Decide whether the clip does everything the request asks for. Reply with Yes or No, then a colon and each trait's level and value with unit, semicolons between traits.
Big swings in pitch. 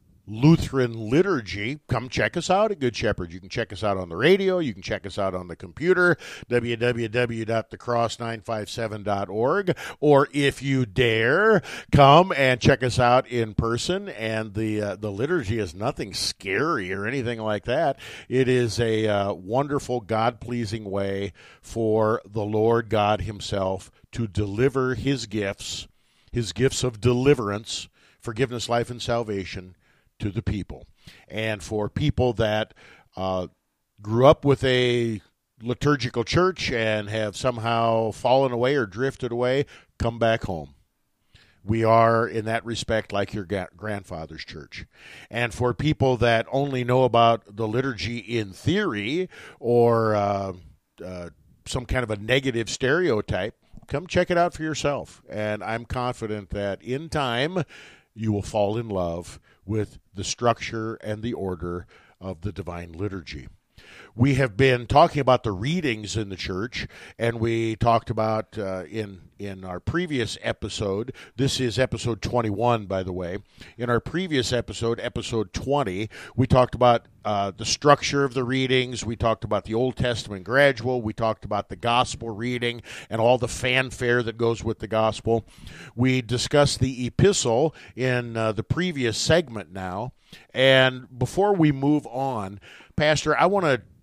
No: average, 3.5 semitones